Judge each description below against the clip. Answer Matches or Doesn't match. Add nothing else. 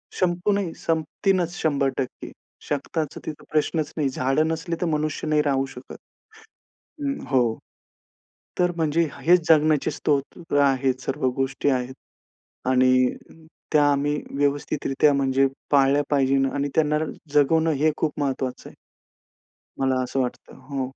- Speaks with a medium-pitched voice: Matches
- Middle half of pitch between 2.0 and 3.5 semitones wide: Matches